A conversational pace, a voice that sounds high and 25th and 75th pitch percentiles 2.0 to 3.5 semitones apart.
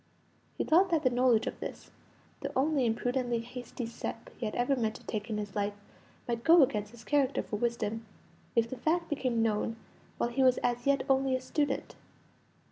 Yes: average, 190 wpm; high, 245 Hz; average, 3.0 semitones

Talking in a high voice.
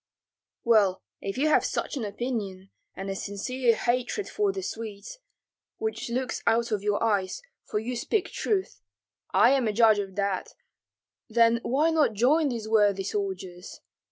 Yes: high, 225 Hz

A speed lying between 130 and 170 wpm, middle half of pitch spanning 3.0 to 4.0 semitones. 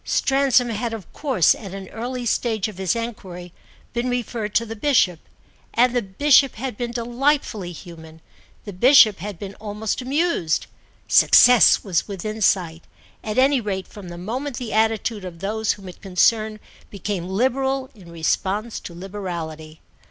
No: average, 155 wpm; average, 4.6 semitones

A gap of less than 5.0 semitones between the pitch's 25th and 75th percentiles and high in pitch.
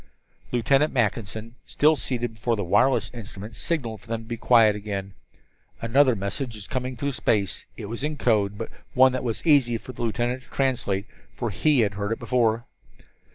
No: average, 3.2 semitones; low, 115 Hz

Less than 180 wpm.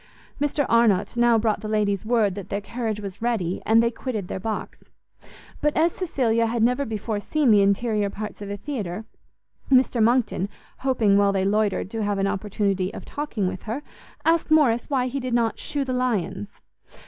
No: average, 185 wpm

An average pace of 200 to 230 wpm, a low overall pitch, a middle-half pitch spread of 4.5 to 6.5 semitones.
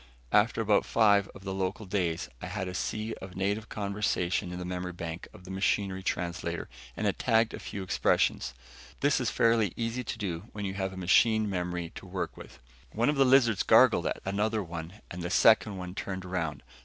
No: fast, 205 wpm; very low, 95 Hz; average, 3.2 semitones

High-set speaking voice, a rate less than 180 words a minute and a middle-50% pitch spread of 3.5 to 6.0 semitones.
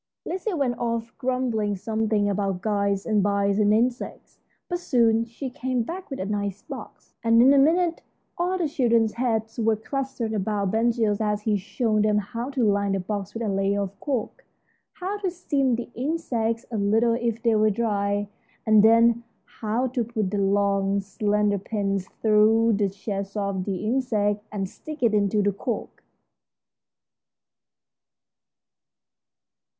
No: high, 220 Hz; average, 160 wpm; average, 3.0 semitones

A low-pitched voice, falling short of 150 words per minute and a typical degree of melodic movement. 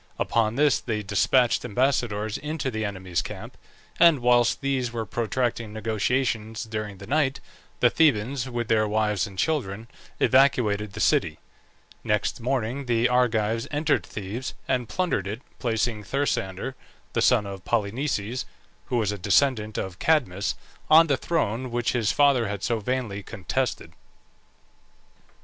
Yes: low, 115 Hz; average, 140 wpm; average, 3.8 semitones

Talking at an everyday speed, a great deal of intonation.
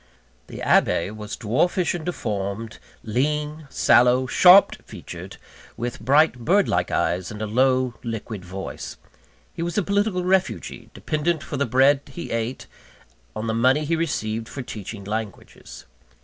Yes: average, 145 wpm; wide, 6.2 semitones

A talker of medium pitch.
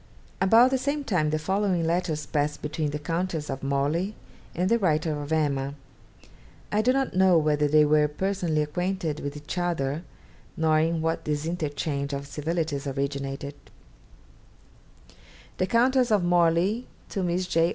Yes: medium, 160 Hz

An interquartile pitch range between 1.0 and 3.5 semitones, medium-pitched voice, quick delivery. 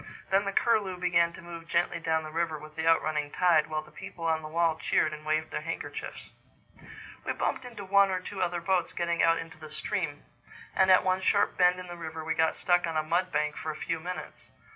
Yes: narrow, 2.5 semitones; medium, 165 Hz; fast, 235 wpm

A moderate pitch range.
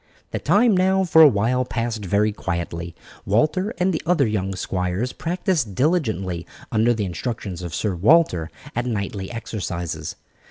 No: wide, 8.6 semitones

